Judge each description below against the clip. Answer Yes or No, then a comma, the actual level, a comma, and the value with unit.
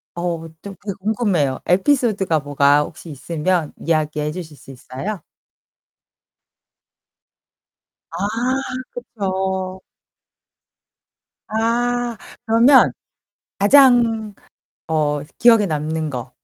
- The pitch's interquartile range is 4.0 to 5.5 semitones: No, wide, 6.4 semitones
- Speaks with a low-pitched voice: No, medium, 185 Hz